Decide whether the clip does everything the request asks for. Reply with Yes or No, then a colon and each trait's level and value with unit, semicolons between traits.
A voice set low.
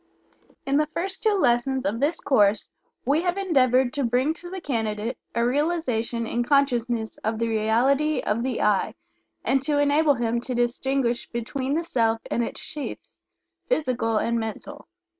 No: very high, 255 Hz